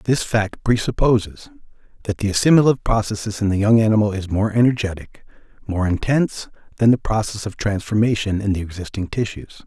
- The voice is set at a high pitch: No, low, 105 Hz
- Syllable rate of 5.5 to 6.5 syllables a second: Yes, 5.9 syllables/s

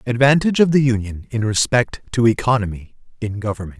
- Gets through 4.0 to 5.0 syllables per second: No, 6.0 syllables/s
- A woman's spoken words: No, male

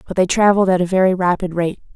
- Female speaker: Yes, female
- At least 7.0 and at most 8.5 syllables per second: Yes, 7.1 syllables/s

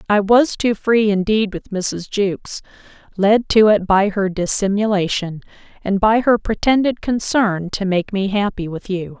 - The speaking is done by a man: No, female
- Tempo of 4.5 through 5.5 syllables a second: No, 4.3 syllables/s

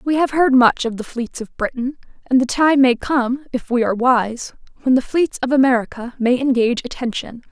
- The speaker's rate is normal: No, fast, 210 wpm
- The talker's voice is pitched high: Yes, very high, 255 Hz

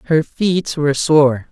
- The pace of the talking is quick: No, average, 160 wpm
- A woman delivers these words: No, male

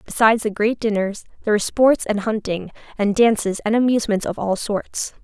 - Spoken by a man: No, female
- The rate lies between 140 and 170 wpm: No, average, 185 wpm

